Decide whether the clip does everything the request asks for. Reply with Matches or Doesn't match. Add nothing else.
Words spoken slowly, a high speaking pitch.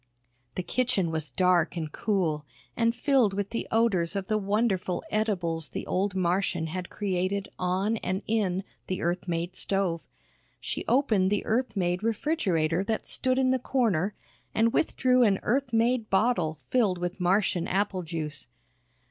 Doesn't match